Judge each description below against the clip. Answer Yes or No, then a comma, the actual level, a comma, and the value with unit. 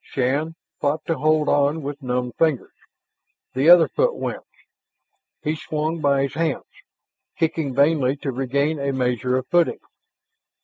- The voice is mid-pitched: Yes, medium, 145 Hz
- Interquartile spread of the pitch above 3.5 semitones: No, average, 3.1 semitones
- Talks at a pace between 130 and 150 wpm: Yes, average, 140 wpm